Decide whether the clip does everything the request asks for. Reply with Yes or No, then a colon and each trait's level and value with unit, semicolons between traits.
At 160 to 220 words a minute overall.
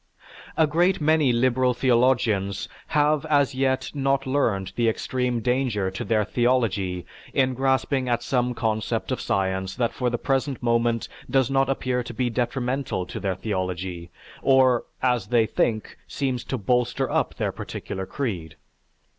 No: average, 150 wpm